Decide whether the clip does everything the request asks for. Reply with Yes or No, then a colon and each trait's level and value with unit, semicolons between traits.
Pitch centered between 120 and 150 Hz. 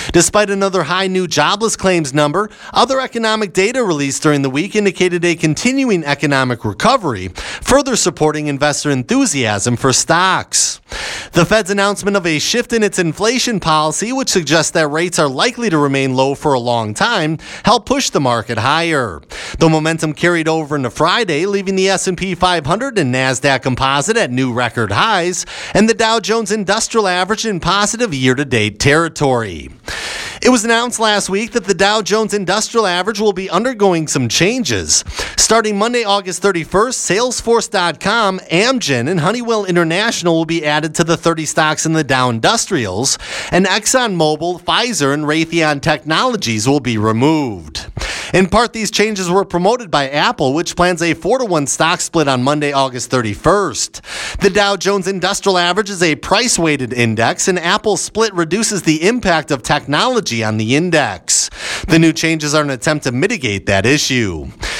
No: medium, 170 Hz